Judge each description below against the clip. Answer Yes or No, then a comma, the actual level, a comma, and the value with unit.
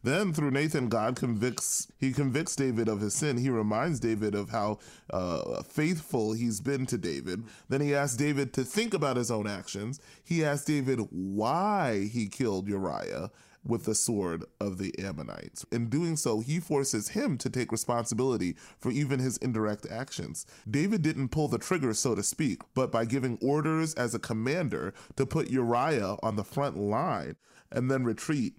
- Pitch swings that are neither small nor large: Yes, average, 4.6 semitones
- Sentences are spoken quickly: No, average, 175 wpm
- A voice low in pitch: Yes, low, 125 Hz